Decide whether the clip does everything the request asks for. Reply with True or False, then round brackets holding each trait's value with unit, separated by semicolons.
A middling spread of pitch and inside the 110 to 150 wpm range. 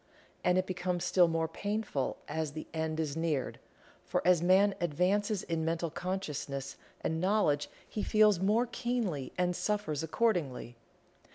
True (4.1 semitones; 145 wpm)